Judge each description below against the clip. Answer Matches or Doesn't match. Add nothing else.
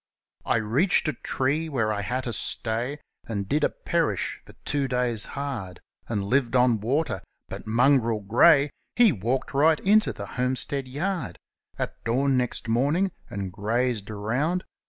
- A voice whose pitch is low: Matches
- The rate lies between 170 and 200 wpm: Doesn't match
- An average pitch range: Matches